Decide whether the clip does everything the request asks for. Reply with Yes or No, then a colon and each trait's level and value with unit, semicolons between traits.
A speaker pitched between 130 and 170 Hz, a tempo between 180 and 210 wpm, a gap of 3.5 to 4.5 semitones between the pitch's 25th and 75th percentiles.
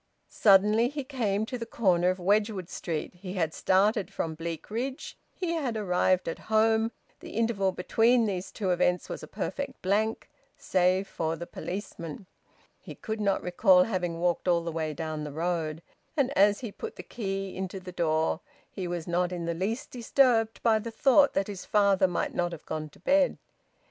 No: high, 190 Hz; average, 185 wpm; average, 4.1 semitones